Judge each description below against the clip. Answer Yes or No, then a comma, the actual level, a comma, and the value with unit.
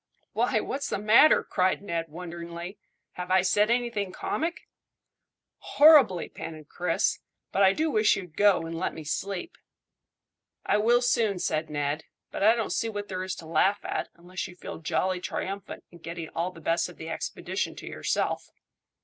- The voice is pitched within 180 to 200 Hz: Yes, medium, 185 Hz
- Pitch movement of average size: Yes, average, 3.9 semitones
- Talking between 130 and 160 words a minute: No, average, 175 wpm